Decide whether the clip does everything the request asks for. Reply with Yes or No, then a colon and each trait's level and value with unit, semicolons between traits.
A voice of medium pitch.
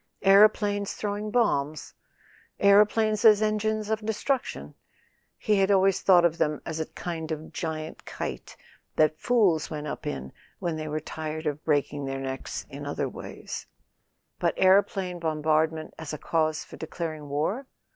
Yes: medium, 165 Hz